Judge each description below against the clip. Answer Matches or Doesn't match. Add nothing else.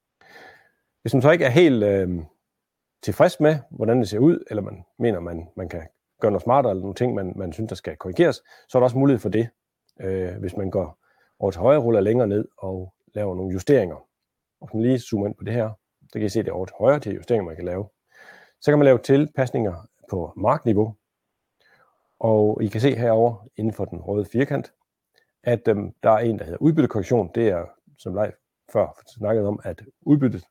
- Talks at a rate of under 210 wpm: Doesn't match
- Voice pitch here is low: Matches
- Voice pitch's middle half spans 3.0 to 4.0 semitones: Doesn't match